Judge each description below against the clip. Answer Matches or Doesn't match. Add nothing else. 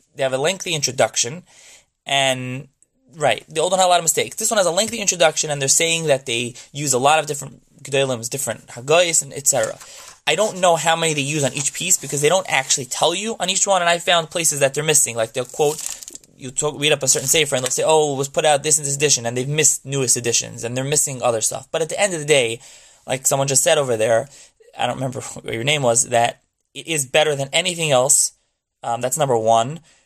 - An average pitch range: Matches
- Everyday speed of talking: Doesn't match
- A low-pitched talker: Doesn't match